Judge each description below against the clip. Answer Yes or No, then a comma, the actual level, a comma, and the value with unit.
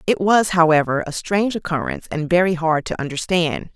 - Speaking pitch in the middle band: Yes, medium, 170 Hz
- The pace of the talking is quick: No, average, 175 wpm